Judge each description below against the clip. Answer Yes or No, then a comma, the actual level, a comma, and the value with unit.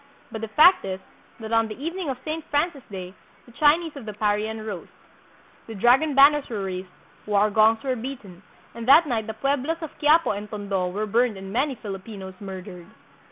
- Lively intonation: Yes, wide, 5.7 semitones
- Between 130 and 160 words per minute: No, average, 190 wpm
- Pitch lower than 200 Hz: No, high, 225 Hz